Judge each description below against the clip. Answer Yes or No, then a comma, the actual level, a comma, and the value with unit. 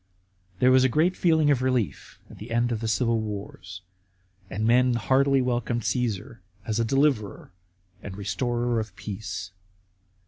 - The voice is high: No, low, 115 Hz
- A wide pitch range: No, average, 3.5 semitones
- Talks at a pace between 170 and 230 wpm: No, average, 150 wpm